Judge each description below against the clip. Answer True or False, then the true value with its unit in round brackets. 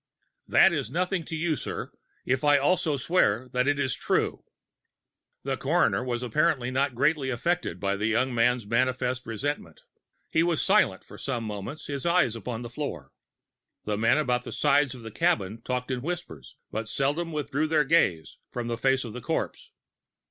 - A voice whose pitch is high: False (130 Hz)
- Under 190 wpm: True (175 wpm)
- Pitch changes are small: False (4.6 semitones)